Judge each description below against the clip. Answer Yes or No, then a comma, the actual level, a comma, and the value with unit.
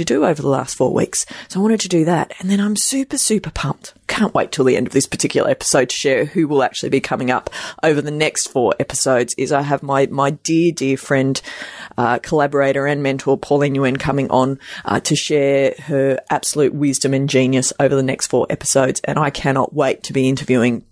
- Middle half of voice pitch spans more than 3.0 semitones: No, narrow, 2.4 semitones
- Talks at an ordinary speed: No, fast, 220 wpm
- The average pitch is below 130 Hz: No, medium, 140 Hz